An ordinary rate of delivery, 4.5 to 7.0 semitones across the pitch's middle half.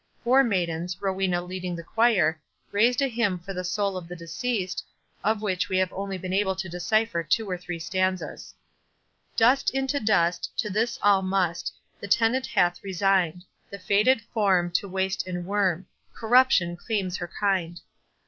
No: average, 165 wpm; average, 3.3 semitones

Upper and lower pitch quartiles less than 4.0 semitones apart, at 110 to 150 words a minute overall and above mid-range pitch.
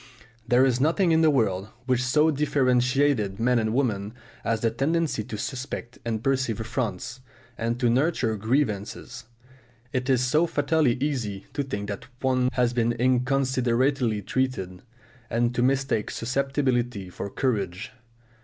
No: average, 3.2 semitones; average, 140 wpm; low, 125 Hz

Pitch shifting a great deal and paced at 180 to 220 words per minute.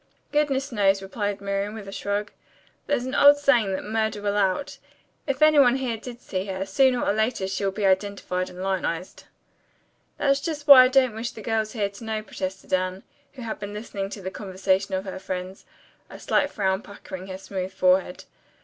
No: average, 4.1 semitones; average, 195 wpm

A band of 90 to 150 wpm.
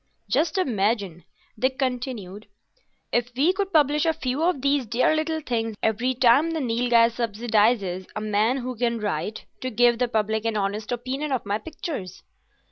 No: average, 165 wpm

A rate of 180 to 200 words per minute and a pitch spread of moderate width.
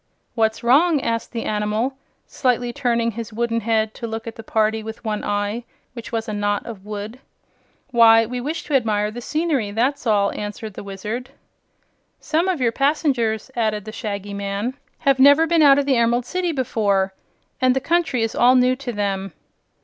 Yes: average, 185 wpm; average, 3.5 semitones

